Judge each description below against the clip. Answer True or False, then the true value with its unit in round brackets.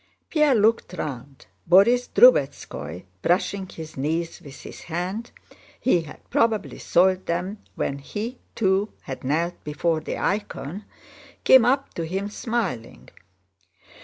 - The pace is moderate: False (125 wpm)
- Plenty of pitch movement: True (5.7 semitones)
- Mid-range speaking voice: True (180 Hz)